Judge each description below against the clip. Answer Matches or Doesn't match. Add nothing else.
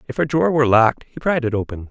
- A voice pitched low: Matches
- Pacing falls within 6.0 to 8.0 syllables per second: Matches